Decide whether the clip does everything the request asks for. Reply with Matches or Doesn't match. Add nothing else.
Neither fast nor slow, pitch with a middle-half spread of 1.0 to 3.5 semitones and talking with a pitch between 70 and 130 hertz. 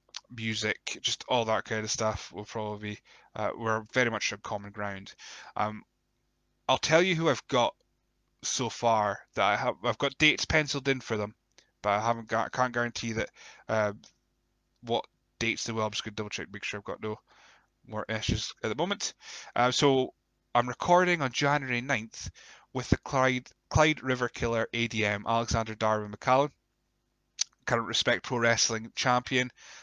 Matches